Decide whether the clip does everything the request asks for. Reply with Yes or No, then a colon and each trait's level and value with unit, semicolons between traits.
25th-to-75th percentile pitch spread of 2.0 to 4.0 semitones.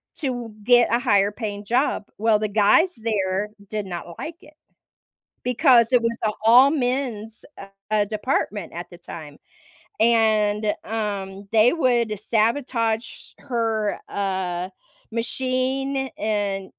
Yes: average, 3.2 semitones